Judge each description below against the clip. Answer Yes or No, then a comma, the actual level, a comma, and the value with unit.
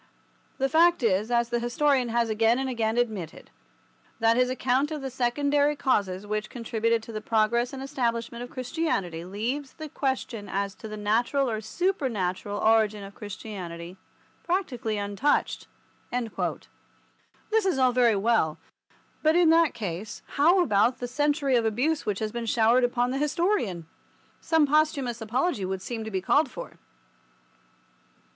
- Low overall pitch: No, high, 235 Hz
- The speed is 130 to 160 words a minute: Yes, average, 150 wpm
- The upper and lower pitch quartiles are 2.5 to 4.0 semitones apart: No, average, 4.5 semitones